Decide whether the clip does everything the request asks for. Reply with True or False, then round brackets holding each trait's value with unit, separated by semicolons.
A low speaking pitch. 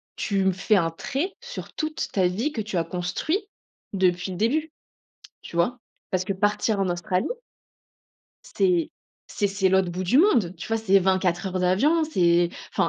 False (195 Hz)